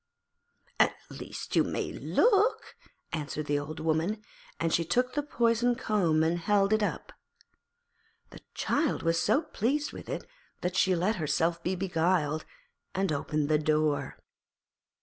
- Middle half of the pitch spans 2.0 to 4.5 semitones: No, wide, 5.6 semitones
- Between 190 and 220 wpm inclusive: No, average, 145 wpm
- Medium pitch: Yes, medium, 175 Hz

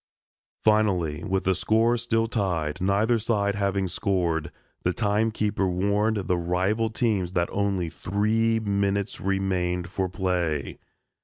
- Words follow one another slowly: Yes, slow, 130 wpm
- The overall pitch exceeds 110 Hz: No, low, 100 Hz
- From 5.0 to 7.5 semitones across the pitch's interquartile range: No, average, 3.1 semitones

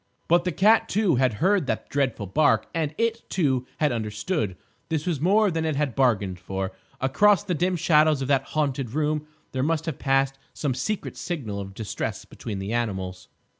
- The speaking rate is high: No, average, 185 wpm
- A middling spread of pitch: No, wide, 5.8 semitones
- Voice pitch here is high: No, medium, 140 Hz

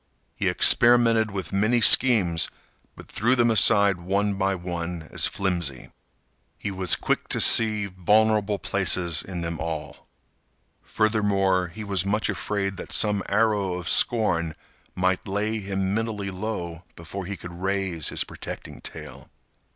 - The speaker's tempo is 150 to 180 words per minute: No, average, 140 wpm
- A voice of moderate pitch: No, low, 100 Hz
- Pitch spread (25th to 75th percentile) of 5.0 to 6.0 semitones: No, average, 3.1 semitones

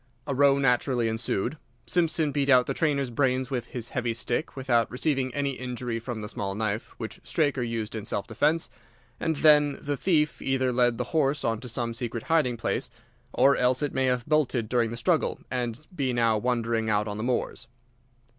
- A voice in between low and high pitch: No, low, 125 Hz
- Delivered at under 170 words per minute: No, average, 195 wpm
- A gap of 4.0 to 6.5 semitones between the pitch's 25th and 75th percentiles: No, average, 3.3 semitones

